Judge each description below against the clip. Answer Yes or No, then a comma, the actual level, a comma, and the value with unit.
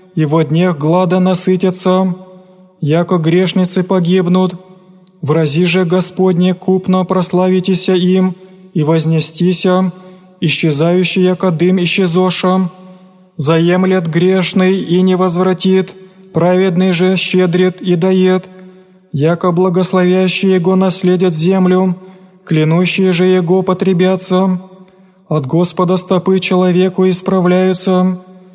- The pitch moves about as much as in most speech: No, narrow, 0.6 semitones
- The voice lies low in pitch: No, medium, 185 Hz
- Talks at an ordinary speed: No, slow, 90 wpm